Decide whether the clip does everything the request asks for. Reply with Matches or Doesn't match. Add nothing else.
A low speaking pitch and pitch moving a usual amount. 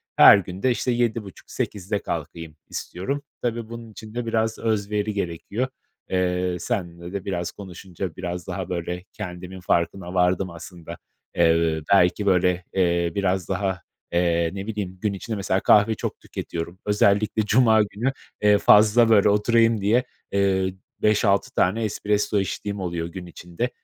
Matches